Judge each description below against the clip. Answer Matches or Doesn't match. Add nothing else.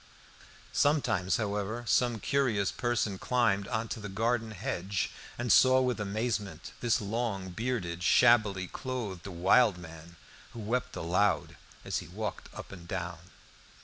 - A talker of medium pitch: Doesn't match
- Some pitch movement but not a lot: Matches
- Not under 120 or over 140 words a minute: Matches